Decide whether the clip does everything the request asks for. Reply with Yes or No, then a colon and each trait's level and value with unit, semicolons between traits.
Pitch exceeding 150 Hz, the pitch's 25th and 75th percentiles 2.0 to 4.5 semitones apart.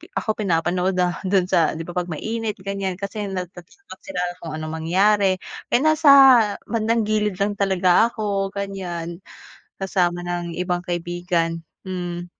Yes: medium, 185 Hz; narrow, 2.6 semitones